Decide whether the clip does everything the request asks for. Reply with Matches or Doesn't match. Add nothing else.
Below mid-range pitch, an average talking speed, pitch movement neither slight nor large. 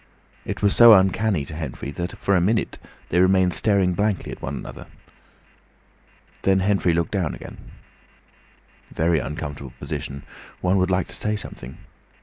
Matches